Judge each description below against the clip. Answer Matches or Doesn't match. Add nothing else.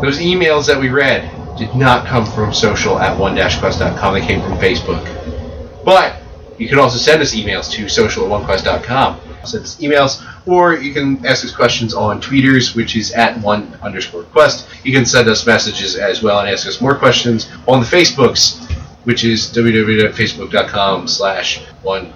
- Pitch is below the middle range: Matches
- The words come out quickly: Doesn't match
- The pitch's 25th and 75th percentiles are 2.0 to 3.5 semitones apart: Doesn't match